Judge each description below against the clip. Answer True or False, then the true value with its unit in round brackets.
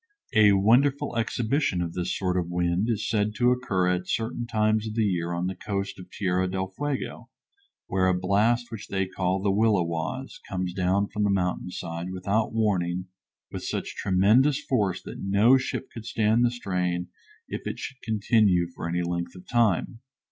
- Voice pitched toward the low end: True (100 Hz)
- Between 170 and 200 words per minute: True (180 wpm)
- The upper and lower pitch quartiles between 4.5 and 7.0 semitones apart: False (3.8 semitones)